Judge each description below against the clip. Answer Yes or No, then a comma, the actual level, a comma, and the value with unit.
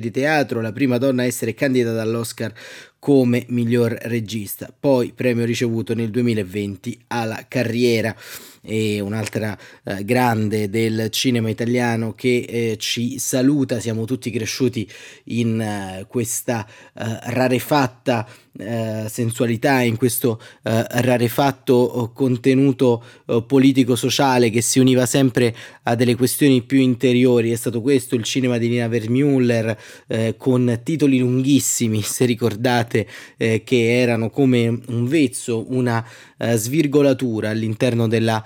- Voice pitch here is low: Yes, low, 120 Hz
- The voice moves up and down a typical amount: No, narrow, 2.2 semitones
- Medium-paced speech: No, slow, 110 wpm